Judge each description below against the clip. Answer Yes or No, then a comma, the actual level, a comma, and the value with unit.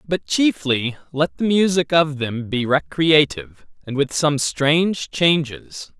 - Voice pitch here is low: No, medium, 145 Hz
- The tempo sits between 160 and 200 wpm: No, average, 140 wpm